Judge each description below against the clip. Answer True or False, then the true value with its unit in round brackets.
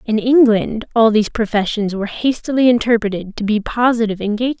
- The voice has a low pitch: False (225 Hz)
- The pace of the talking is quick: False (155 wpm)